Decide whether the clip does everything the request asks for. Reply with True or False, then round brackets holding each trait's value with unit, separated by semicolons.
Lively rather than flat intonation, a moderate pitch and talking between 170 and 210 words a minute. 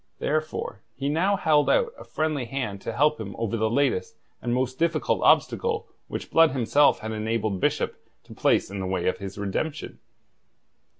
False (6.3 semitones; 130 Hz; 175 wpm)